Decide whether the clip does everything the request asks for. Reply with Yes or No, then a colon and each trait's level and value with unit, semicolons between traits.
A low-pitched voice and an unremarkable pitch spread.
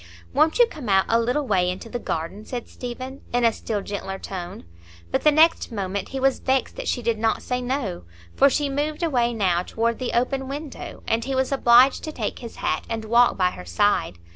No: high, 240 Hz; average, 4.7 semitones